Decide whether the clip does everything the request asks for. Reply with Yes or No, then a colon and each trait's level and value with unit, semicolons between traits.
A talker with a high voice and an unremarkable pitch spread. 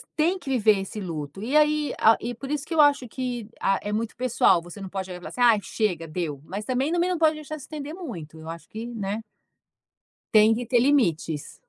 No: high, 225 Hz; wide, 7.0 semitones